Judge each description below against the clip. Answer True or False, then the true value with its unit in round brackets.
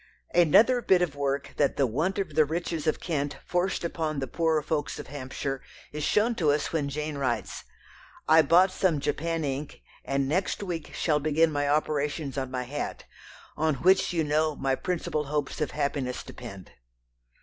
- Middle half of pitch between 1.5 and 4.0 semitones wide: True (2.9 semitones)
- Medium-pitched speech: True (150 Hz)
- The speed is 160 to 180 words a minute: True (175 wpm)